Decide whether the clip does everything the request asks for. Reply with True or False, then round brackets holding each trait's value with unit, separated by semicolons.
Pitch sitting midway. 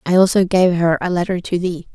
True (180 Hz)